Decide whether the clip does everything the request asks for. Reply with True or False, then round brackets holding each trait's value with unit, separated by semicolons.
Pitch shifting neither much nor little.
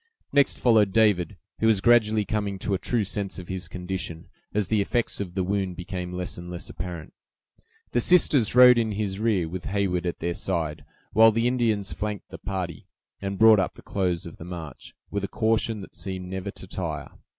True (3.3 semitones)